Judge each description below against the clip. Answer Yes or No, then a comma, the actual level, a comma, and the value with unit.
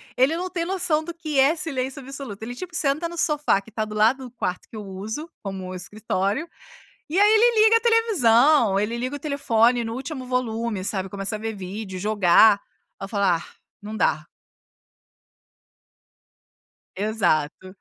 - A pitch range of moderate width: No, wide, 7.0 semitones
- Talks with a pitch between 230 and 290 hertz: Yes, high, 235 Hz